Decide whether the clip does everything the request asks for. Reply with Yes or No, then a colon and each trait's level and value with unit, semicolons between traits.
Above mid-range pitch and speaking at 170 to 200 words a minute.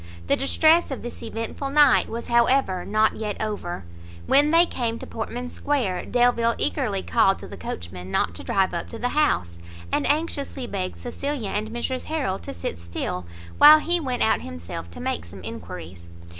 Yes: high, 225 Hz; average, 180 wpm